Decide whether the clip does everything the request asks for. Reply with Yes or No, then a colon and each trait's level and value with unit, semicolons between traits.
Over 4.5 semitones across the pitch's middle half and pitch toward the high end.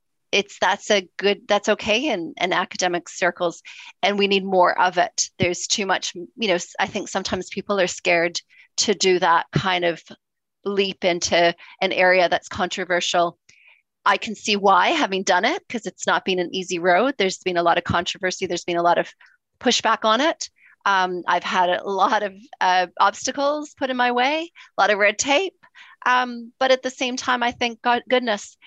Yes: average, 5.2 semitones; high, 195 Hz